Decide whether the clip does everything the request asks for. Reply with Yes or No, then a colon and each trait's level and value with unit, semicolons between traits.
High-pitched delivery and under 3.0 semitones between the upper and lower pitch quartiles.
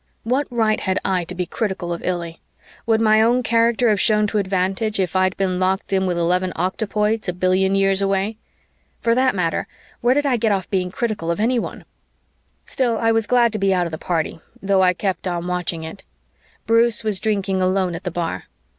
No: high, 195 Hz; average, 3.4 semitones